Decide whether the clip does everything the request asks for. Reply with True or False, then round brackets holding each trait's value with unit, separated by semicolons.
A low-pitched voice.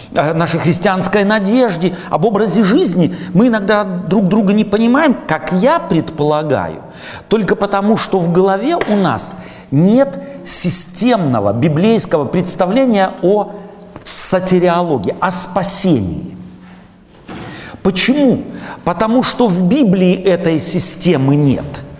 False (185 Hz)